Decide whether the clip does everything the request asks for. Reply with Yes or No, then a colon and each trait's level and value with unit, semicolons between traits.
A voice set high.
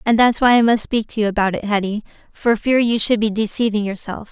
Yes: high, 220 Hz